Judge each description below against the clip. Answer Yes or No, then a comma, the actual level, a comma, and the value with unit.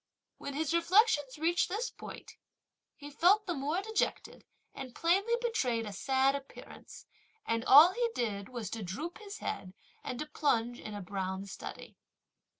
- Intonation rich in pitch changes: Yes, wide, 7.8 semitones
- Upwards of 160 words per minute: No, average, 155 wpm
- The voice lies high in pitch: Yes, very high, 280 Hz